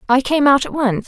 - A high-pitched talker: Yes, very high, 265 Hz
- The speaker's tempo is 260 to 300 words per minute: Yes, fast, 280 wpm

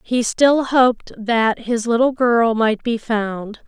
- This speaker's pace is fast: No, average, 165 wpm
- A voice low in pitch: No, high, 230 Hz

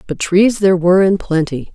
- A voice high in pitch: No, medium, 180 Hz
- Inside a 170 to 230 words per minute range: Yes, fast, 205 wpm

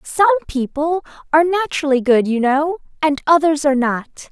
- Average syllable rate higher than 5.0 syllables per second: Yes, 5.3 syllables/s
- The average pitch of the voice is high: Yes, very high, 300 Hz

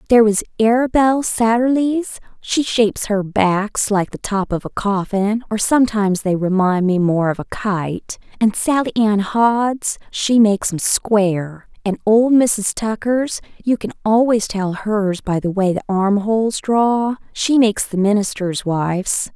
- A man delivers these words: No, female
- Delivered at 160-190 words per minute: No, average, 150 wpm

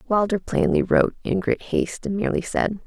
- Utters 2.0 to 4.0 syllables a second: No, 5.8 syllables/s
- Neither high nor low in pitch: No, high, 200 Hz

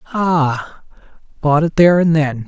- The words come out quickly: No, average, 145 wpm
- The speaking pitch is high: No, medium, 155 Hz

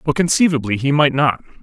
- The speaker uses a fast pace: No, average, 185 wpm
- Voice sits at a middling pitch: Yes, medium, 145 Hz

